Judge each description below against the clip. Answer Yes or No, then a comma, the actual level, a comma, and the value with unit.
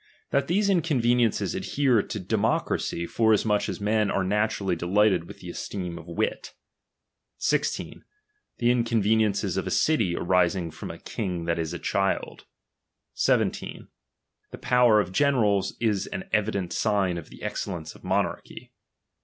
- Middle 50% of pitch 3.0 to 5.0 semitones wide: Yes, average, 4.1 semitones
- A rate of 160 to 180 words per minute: No, average, 145 wpm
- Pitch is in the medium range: No, low, 105 Hz